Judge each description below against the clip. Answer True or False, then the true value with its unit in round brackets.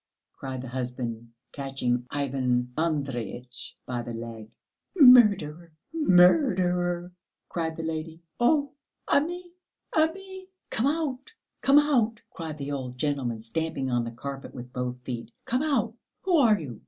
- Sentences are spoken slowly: True (130 wpm)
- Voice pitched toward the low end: False (155 Hz)